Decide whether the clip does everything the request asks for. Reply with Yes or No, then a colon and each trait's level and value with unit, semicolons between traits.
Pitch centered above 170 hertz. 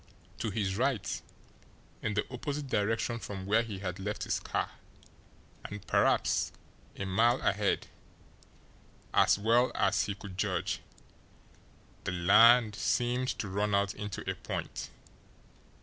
No: low, 105 Hz